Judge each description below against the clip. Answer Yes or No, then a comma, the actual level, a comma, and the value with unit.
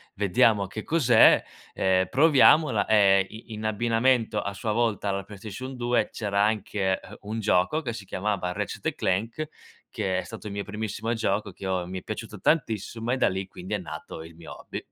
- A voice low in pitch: Yes, low, 105 Hz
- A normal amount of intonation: Yes, average, 3.0 semitones